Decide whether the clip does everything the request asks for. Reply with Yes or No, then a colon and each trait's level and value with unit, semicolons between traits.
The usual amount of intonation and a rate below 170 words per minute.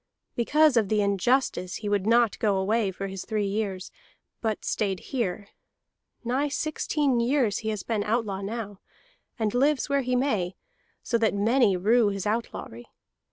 Yes: average, 3.6 semitones; average, 160 wpm